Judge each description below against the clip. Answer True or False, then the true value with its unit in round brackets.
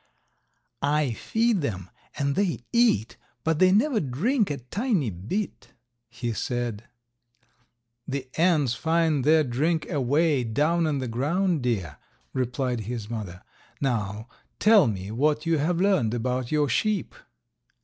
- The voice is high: False (140 Hz)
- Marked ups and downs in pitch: True (6.0 semitones)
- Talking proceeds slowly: True (130 wpm)